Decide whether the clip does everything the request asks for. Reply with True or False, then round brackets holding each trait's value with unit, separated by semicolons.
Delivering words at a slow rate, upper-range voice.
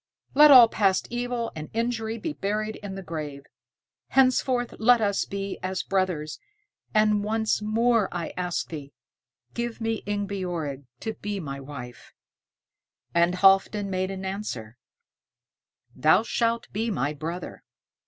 True (130 wpm; 200 Hz)